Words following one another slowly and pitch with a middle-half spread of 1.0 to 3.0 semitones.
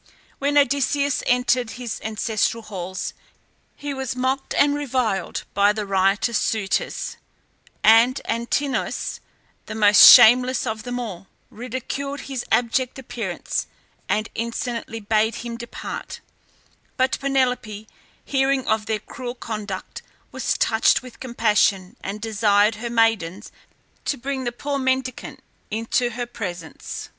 No: slow, 120 wpm; average, 3.4 semitones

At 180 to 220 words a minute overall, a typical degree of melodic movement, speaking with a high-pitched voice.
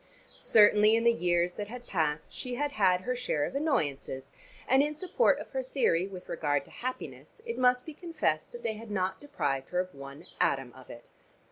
No: fast, 205 wpm; wide, 8.4 semitones; high, 205 Hz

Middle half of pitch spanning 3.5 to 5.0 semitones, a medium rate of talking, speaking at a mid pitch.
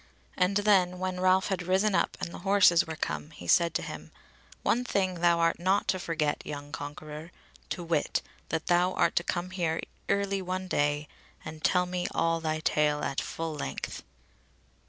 No: average, 2.9 semitones; average, 180 wpm; medium, 175 Hz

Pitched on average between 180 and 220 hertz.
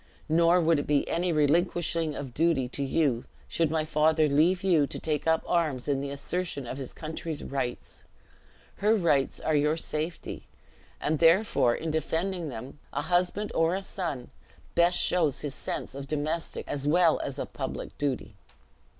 No: medium, 155 Hz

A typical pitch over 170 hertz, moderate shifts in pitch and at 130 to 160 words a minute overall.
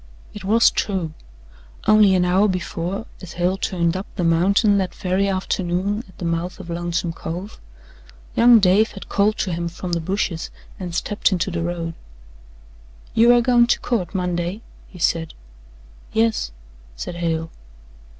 Yes: medium, 185 Hz; average, 3.0 semitones; average, 155 wpm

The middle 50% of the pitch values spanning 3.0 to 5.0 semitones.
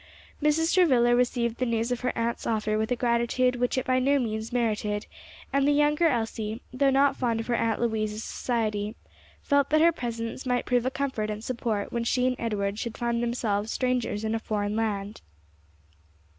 No: narrow, 2.6 semitones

